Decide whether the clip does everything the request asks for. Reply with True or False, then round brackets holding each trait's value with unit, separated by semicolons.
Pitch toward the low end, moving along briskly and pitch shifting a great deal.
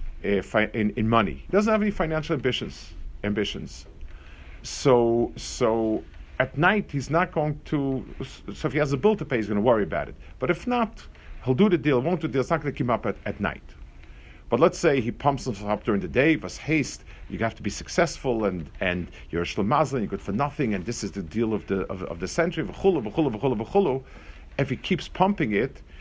True (115 Hz; 225 wpm; 8.7 semitones)